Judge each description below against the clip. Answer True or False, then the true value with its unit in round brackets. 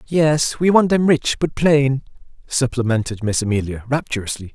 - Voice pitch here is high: False (135 Hz)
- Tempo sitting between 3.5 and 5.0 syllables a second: True (4.9 syllables/s)